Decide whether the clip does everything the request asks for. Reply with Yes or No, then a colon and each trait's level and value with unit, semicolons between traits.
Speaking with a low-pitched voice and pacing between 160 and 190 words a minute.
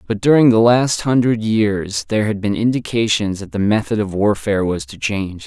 No: low, 105 Hz; average, 200 wpm